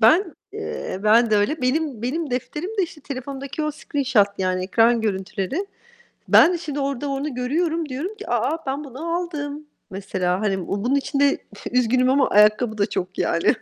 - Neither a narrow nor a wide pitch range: No, wide, 5.8 semitones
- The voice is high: Yes, very high, 265 Hz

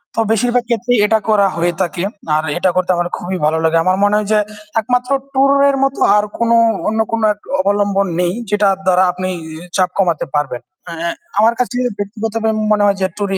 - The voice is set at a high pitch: Yes, high, 200 Hz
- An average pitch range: Yes, average, 3.4 semitones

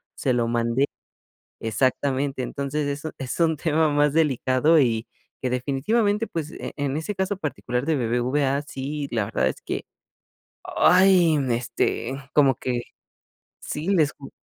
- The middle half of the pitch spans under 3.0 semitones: No, average, 3.7 semitones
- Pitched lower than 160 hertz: Yes, medium, 140 Hz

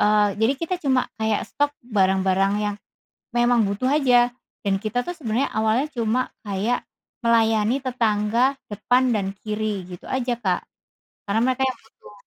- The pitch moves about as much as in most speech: Yes, average, 3.4 semitones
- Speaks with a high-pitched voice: Yes, high, 225 Hz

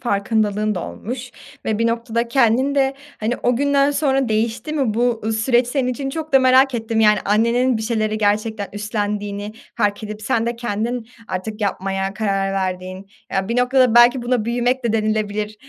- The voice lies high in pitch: Yes, high, 225 Hz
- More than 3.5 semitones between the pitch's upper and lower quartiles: No, average, 2.9 semitones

